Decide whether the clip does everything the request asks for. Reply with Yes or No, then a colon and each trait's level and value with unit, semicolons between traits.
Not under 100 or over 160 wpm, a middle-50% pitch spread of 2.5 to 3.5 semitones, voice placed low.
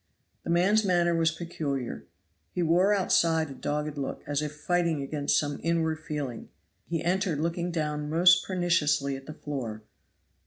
No: average, 155 wpm; average, 2.9 semitones; medium, 160 Hz